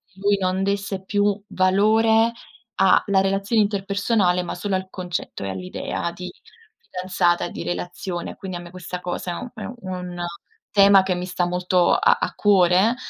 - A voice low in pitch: No, medium, 185 Hz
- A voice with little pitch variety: Yes, narrow, 2.0 semitones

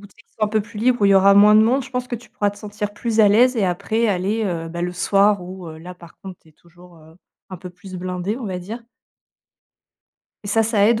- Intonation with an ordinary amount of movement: Yes, average, 3.5 semitones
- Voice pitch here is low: No, high, 200 Hz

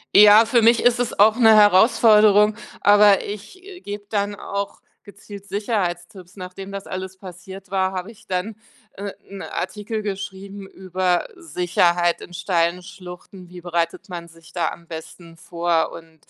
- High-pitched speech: Yes, high, 195 Hz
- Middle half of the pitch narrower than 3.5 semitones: Yes, average, 2.7 semitones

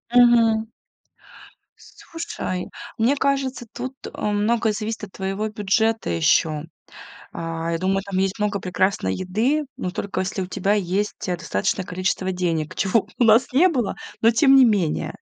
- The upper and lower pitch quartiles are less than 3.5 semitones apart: No, average, 3.8 semitones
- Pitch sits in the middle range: No, high, 205 Hz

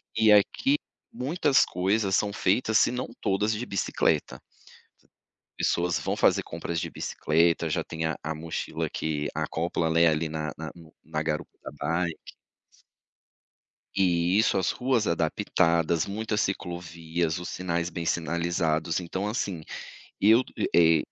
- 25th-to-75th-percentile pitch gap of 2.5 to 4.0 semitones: Yes, average, 3.7 semitones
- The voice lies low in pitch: Yes, very low, 85 Hz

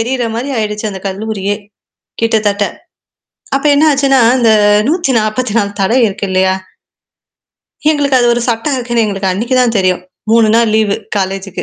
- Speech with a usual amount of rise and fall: Yes, average, 3.7 semitones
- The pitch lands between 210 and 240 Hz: Yes, high, 220 Hz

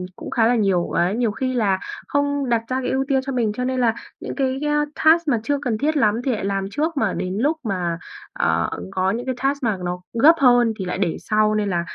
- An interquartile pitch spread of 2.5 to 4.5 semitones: No, average, 5.3 semitones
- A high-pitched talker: Yes, high, 235 Hz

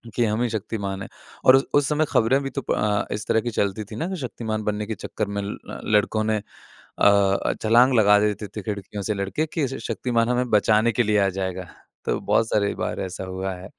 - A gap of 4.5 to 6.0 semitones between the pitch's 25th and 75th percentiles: No, average, 2.7 semitones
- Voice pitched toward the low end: Yes, low, 105 Hz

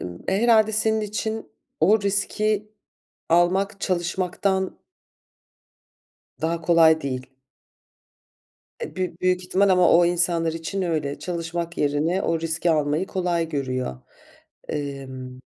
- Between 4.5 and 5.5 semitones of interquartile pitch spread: No, average, 3.3 semitones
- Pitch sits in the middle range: Yes, medium, 170 Hz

